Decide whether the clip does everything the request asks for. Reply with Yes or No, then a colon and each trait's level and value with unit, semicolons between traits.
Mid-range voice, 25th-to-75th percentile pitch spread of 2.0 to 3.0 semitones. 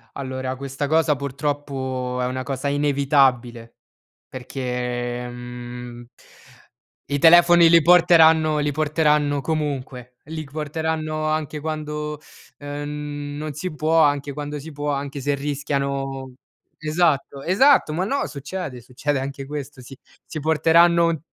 Yes: medium, 145 Hz; average, 2.7 semitones